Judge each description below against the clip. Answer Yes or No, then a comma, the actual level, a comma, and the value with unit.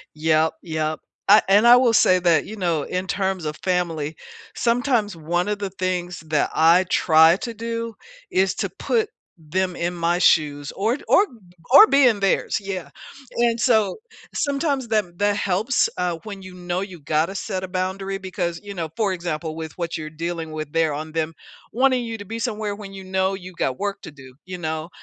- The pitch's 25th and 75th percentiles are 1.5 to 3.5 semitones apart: No, average, 4.1 semitones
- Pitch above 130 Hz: Yes, medium, 185 Hz